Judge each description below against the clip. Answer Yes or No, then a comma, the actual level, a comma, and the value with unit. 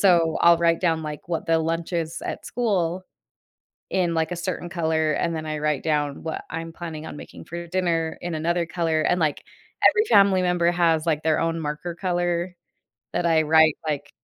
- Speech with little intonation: Yes, narrow, 1.7 semitones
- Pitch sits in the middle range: Yes, medium, 165 Hz